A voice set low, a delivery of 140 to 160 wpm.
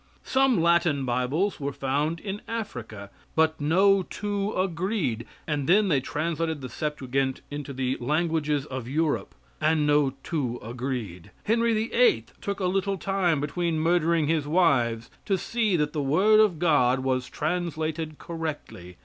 No: medium, 155 Hz; average, 145 wpm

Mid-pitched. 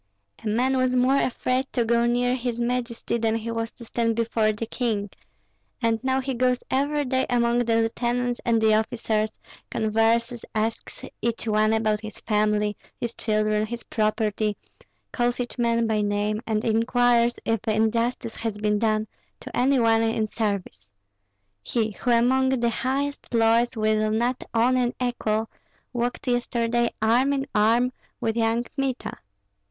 No: high, 230 Hz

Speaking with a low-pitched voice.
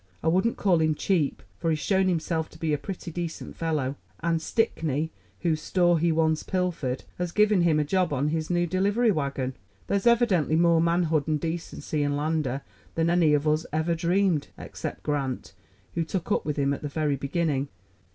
No: medium, 160 Hz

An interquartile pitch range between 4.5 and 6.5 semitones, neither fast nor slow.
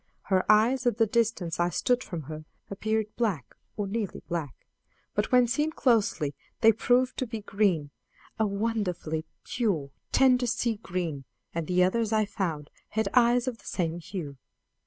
Yes: average, 5.2 semitones; average, 160 wpm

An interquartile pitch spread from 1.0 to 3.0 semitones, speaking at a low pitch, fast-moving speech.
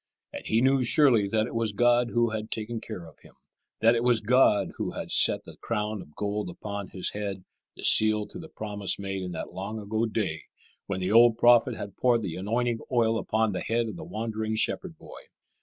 Yes: narrow, 2.5 semitones; low, 110 Hz; fast, 215 wpm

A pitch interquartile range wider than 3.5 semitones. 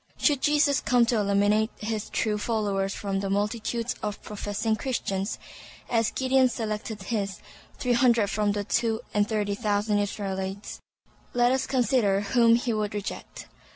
No: average, 2.8 semitones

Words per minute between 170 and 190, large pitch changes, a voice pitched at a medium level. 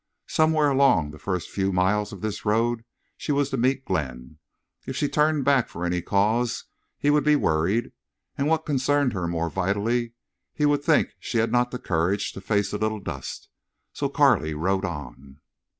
No: average, 180 wpm; wide, 7.3 semitones; low, 110 Hz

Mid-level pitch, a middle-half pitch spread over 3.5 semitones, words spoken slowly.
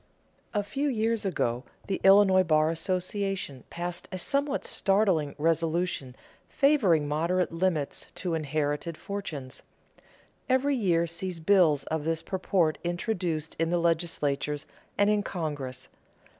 Yes: medium, 170 Hz; average, 4.1 semitones; slow, 120 wpm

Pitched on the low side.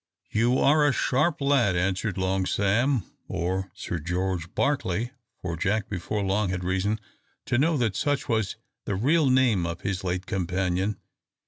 Yes: low, 100 Hz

